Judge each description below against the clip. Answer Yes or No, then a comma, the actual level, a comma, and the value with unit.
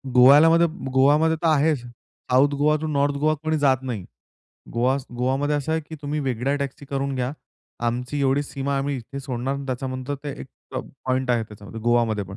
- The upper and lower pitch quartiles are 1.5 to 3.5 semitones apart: Yes, narrow, 2.6 semitones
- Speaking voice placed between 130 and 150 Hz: Yes, low, 135 Hz